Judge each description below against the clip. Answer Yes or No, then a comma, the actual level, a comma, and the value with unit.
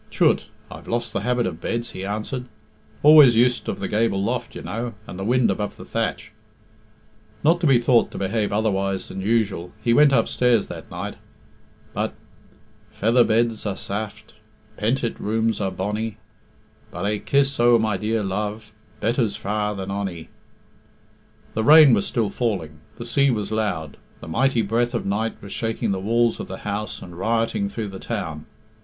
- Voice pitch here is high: No, low, 110 Hz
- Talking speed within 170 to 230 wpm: Yes, average, 175 wpm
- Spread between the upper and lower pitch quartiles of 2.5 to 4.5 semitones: Yes, average, 2.9 semitones